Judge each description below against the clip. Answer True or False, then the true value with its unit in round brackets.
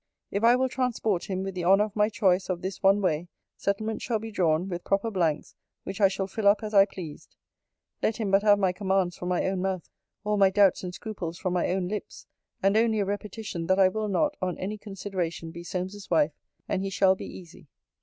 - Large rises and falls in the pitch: False (2.4 semitones)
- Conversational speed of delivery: False (225 wpm)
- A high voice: True (195 Hz)